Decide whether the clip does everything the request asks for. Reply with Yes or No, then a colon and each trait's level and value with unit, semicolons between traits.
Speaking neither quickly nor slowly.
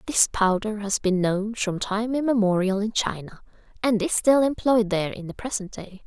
Yes: average, 190 wpm